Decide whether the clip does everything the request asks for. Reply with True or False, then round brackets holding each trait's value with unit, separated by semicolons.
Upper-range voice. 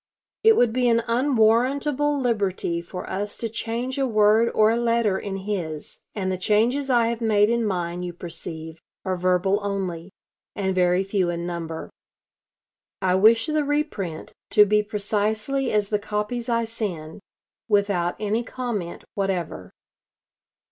True (210 Hz)